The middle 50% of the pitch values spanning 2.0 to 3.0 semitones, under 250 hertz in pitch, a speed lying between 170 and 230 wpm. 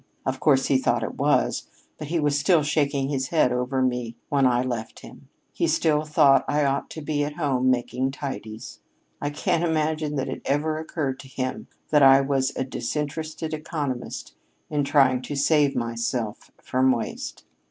Yes: narrow, 2.5 semitones; medium, 140 Hz; average, 175 wpm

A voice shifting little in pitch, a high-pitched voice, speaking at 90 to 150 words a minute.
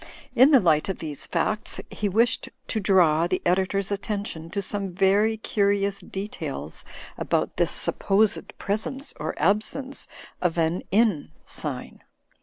No: average, 3.1 semitones; high, 200 Hz; slow, 135 wpm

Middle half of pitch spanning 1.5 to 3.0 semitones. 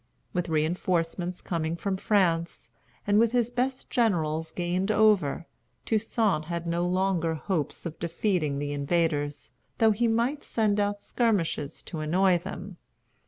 No: average, 4.3 semitones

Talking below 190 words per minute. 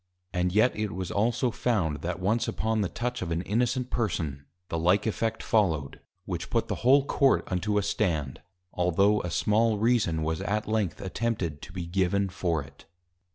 Yes: average, 180 wpm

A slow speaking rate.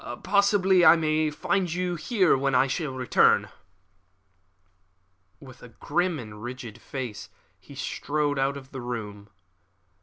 Yes: slow, 125 wpm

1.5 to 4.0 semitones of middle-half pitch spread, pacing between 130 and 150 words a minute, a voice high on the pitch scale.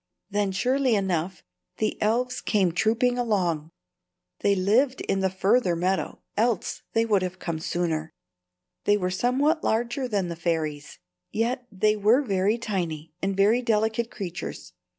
No: average, 4.4 semitones; average, 140 wpm; high, 205 Hz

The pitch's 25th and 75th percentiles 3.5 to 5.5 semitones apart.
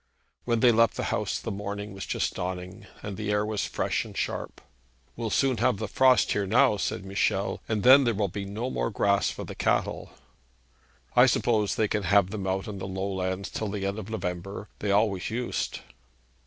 No: narrow, 2.4 semitones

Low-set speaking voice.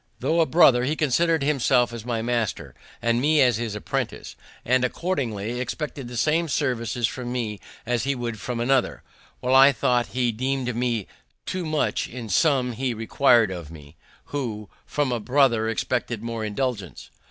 Yes: low, 125 Hz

